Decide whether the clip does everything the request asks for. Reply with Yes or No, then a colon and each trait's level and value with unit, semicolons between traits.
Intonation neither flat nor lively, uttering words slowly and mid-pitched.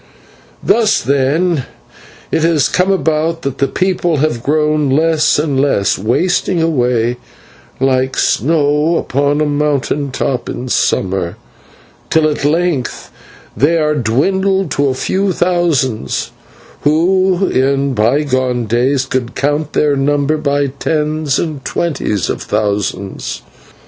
Yes: average, 3.7 semitones; slow, 120 wpm; medium, 145 Hz